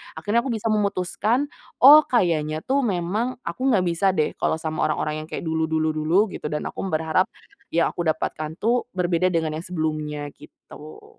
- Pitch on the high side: No, medium, 170 Hz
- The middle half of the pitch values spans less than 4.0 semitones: No, average, 4.8 semitones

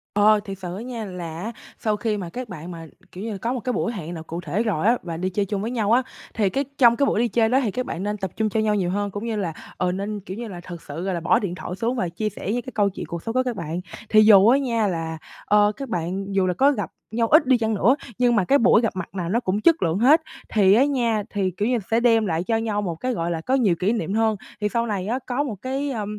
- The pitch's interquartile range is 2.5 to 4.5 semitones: Yes, average, 4.1 semitones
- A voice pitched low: No, high, 210 Hz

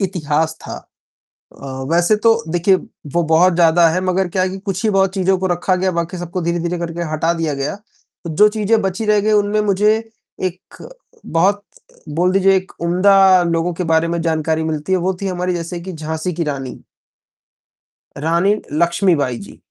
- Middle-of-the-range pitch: Yes, medium, 175 Hz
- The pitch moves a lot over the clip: No, narrow, 2.6 semitones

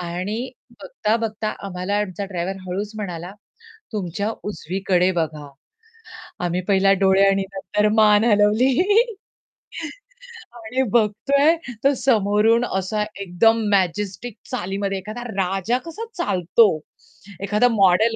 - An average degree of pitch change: Yes, average, 3.2 semitones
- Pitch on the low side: No, high, 205 Hz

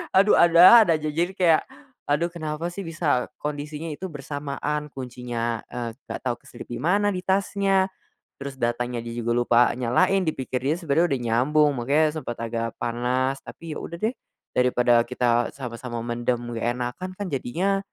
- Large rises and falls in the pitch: Yes, wide, 5.8 semitones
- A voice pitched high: No, medium, 145 Hz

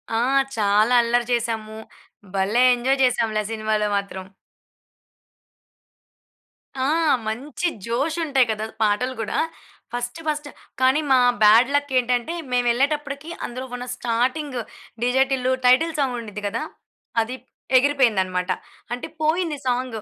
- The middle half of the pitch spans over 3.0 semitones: Yes, average, 3.7 semitones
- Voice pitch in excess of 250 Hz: No, high, 245 Hz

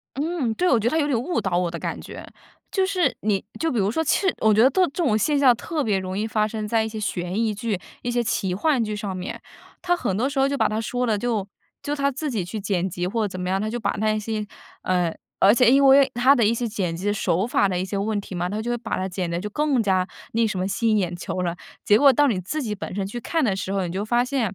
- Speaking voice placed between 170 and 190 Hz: No, high, 215 Hz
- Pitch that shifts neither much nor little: Yes, average, 4.9 semitones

